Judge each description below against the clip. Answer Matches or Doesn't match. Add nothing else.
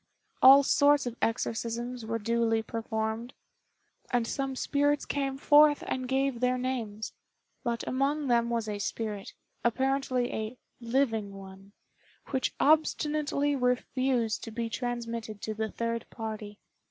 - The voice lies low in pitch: Doesn't match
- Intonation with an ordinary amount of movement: Matches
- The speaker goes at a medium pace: Doesn't match